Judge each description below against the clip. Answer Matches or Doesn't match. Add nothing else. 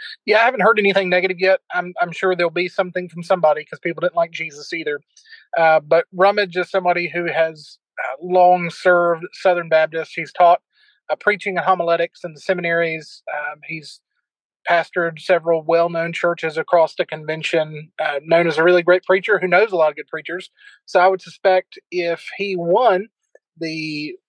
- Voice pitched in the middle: Matches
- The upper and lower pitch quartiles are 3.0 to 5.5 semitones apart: Doesn't match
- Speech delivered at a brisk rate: Doesn't match